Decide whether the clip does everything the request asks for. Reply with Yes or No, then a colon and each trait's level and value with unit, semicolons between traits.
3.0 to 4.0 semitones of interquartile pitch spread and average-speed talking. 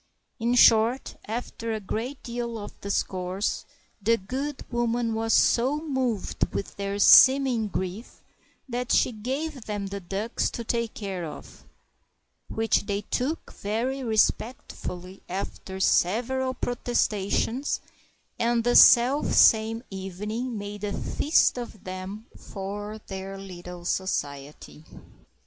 No: average, 3.7 semitones; slow, 115 wpm